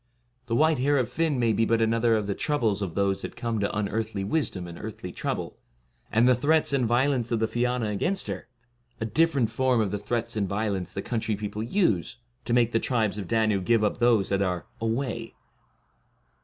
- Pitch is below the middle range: Yes, low, 115 Hz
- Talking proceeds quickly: Yes, fast, 215 wpm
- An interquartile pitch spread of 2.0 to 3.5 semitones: Yes, average, 3.0 semitones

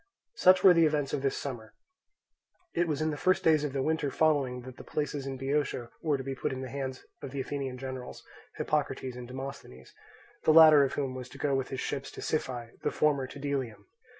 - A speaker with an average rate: No, fast, 220 wpm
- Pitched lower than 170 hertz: Yes, low, 135 Hz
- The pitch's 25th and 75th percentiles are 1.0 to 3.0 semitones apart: Yes, narrow, 2.4 semitones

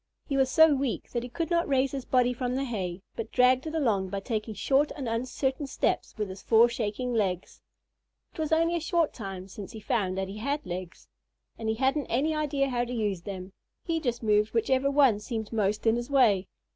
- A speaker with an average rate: No, fast, 220 wpm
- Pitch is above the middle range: Yes, high, 240 Hz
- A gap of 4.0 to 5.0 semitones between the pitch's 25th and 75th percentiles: Yes, average, 4.7 semitones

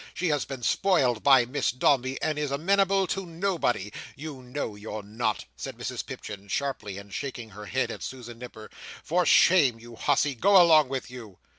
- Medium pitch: No, low, 130 Hz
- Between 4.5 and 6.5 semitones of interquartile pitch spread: Yes, wide, 5.6 semitones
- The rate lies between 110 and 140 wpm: No, average, 180 wpm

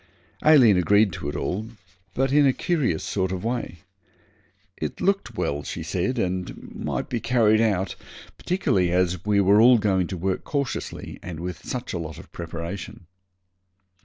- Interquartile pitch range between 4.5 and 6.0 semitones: Yes, average, 5.2 semitones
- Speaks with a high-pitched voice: No, low, 100 Hz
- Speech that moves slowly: No, average, 160 wpm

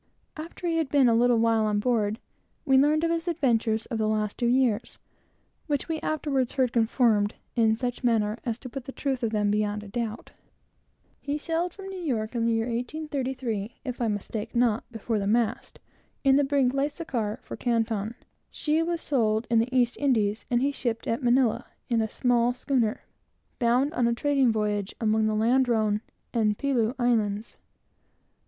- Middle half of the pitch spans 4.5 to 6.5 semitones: No, average, 3.6 semitones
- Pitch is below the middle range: No, high, 240 Hz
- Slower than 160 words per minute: No, average, 185 wpm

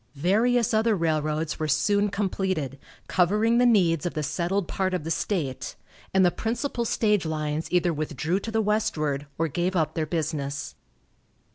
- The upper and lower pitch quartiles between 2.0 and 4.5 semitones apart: No, average, 5.1 semitones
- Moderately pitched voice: Yes, medium, 175 Hz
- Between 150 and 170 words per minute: Yes, average, 160 wpm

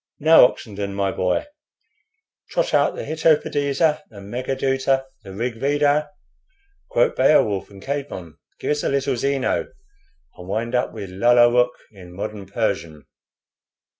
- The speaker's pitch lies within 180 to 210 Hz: No, low, 120 Hz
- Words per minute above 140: No, slow, 135 wpm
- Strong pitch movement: Yes, wide, 5.8 semitones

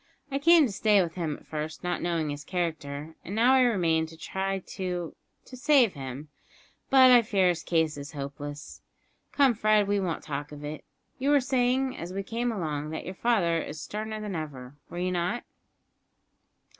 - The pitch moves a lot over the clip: Yes, wide, 6.5 semitones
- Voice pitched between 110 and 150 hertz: No, medium, 180 Hz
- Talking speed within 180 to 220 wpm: Yes, average, 190 wpm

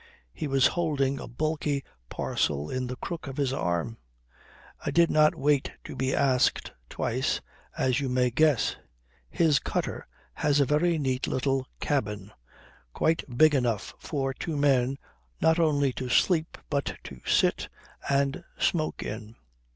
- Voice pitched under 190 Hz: Yes, low, 135 Hz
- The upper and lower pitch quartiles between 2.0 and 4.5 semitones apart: Yes, average, 3.2 semitones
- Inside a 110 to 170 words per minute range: Yes, average, 145 wpm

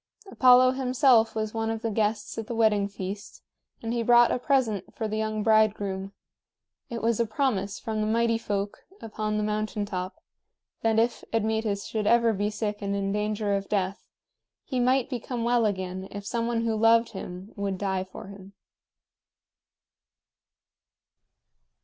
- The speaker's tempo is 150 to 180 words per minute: Yes, average, 160 wpm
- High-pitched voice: Yes, high, 215 Hz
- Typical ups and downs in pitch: No, narrow, 2.3 semitones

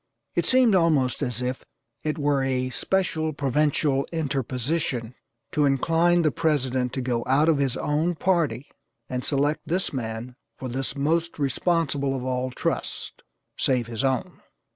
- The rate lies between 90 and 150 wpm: Yes, average, 145 wpm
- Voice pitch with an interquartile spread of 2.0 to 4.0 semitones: Yes, average, 3.7 semitones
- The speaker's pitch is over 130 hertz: Yes, medium, 140 Hz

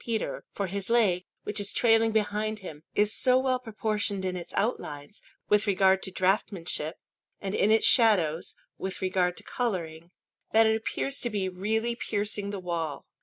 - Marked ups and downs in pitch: No, average, 3.3 semitones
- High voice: Yes, high, 205 Hz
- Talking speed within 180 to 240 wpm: No, average, 170 wpm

